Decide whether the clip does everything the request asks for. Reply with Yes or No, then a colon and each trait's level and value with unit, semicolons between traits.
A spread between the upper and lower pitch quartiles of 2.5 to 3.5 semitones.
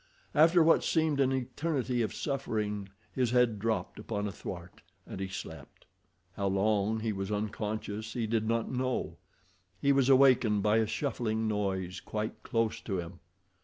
No: average, 4.0 semitones